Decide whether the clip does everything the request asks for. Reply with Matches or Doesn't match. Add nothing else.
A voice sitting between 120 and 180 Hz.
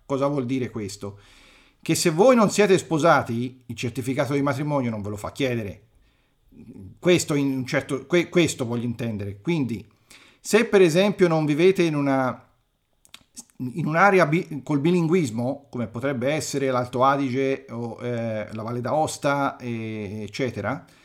Matches